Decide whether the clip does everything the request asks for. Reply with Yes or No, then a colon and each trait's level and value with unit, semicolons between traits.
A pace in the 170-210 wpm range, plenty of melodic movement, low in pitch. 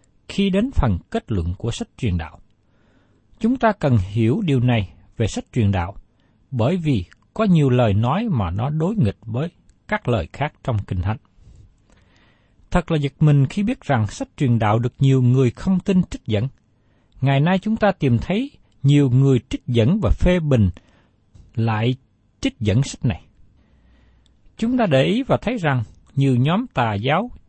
Yes: average, 180 wpm; wide, 6.8 semitones; low, 120 Hz